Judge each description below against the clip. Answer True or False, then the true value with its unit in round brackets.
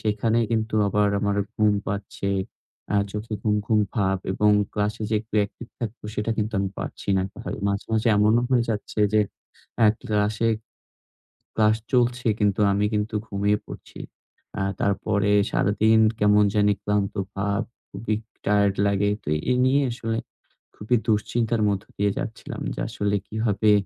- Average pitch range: False (1.4 semitones)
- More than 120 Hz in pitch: False (105 Hz)